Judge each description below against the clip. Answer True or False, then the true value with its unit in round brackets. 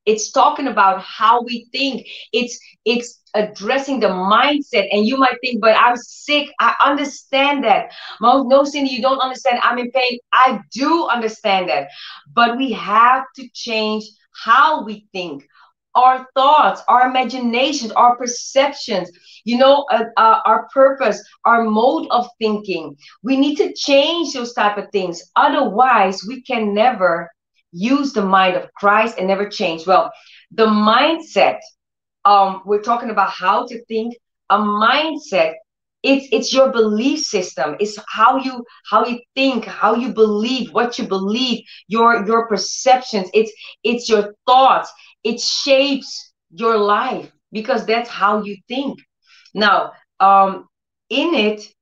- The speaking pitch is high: True (235 Hz)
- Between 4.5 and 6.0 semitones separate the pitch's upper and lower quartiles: False (4.0 semitones)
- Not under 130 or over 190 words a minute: True (145 wpm)